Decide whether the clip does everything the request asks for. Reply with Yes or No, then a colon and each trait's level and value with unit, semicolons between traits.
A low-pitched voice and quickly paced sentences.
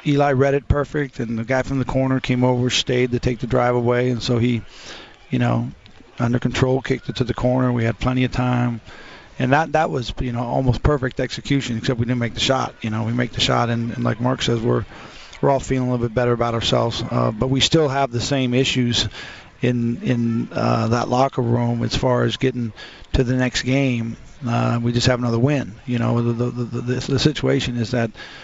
Yes: low, 125 Hz; fast, 230 wpm